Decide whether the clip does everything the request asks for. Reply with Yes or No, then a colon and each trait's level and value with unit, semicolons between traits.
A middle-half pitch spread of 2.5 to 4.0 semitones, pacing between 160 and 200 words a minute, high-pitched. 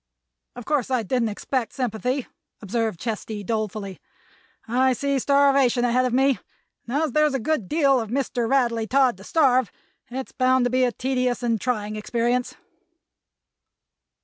No: average, 2.8 semitones; average, 150 wpm; very high, 250 Hz